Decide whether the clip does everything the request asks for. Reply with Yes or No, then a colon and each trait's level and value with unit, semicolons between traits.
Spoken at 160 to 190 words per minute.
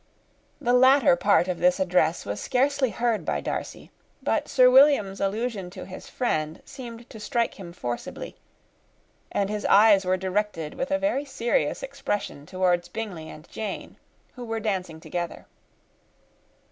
No: average, 150 wpm